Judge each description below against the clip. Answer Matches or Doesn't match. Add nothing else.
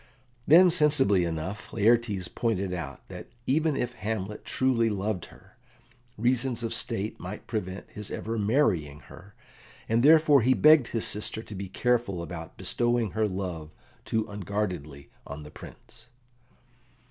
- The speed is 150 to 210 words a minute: Doesn't match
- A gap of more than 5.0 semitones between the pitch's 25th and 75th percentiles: Doesn't match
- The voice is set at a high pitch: Doesn't match